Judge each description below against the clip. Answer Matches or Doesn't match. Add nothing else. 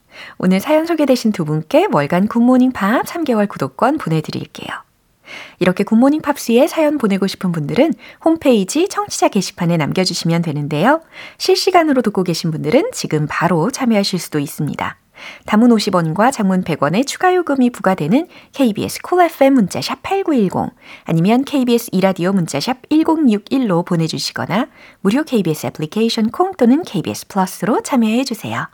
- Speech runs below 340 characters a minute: Doesn't match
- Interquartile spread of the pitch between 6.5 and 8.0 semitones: Matches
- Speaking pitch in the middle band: Doesn't match